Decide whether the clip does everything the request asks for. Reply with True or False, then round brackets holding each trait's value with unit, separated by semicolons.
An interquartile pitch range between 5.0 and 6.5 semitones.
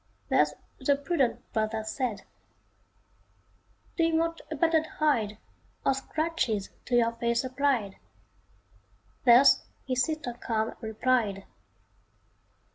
True (5.5 semitones)